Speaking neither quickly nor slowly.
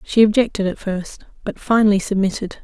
Yes: average, 160 wpm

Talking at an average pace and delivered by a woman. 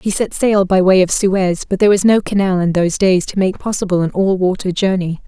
No: fast, 250 wpm; female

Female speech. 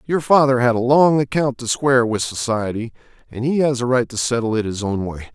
No: male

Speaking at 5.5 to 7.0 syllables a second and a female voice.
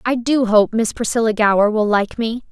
No: 5.1 syllables/s; female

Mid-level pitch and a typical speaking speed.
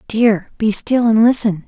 No: high, 220 Hz; average, 180 wpm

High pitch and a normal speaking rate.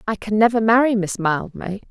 Yes: high, 215 Hz; average, 190 wpm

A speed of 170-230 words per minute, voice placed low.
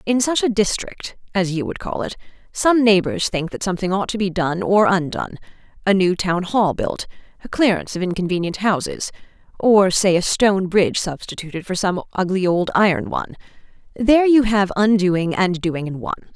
No: average, 180 wpm; high, 190 Hz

